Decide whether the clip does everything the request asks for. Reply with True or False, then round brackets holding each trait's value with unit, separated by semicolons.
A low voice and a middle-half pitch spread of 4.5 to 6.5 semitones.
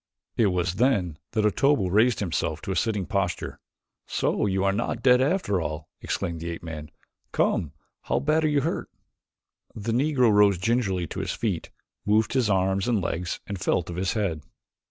True (100 Hz; 5.1 semitones)